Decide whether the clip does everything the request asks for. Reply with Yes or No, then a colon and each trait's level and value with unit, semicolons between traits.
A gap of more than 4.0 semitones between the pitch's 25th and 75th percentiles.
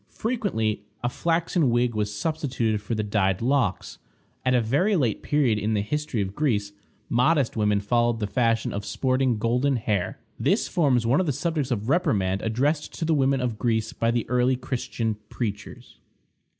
Yes: average, 4.5 semitones